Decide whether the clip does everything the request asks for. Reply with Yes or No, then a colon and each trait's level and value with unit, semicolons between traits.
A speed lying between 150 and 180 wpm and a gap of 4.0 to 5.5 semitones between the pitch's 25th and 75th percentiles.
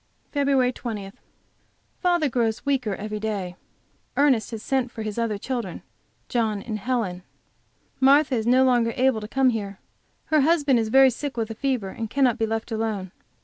No: average, 170 wpm; average, 3.5 semitones